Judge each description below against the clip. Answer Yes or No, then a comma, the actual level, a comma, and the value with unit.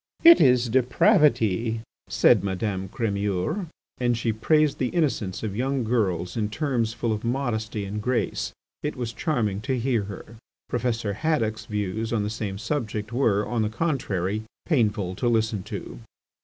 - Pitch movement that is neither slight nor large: Yes, average, 3.4 semitones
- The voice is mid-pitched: No, low, 110 Hz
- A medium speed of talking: Yes, average, 155 wpm